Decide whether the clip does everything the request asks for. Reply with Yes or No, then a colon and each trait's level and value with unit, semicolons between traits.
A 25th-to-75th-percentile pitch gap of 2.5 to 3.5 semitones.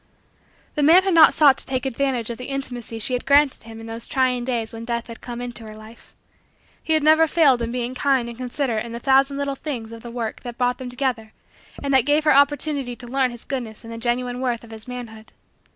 Yes: average, 2.8 semitones